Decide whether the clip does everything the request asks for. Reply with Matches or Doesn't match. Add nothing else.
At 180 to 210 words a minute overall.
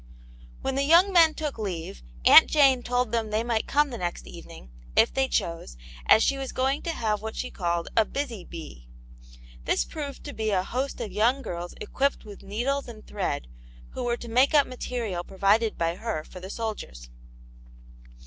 Matches